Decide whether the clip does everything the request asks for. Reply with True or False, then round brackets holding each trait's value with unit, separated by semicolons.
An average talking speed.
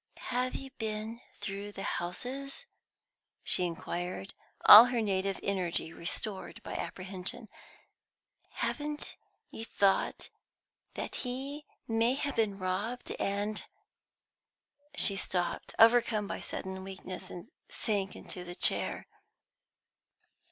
False (110 wpm)